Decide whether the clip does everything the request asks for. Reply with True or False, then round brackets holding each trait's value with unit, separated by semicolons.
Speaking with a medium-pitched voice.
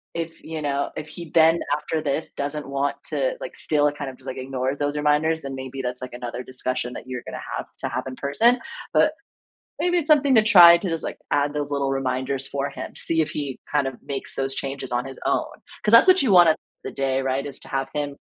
True (145 Hz)